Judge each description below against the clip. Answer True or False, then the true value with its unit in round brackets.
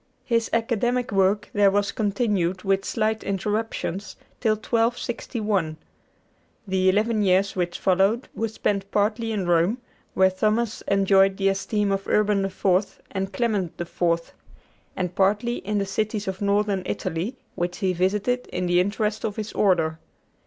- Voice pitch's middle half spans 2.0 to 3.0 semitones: True (2.4 semitones)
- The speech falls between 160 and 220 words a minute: False (145 wpm)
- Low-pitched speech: False (200 Hz)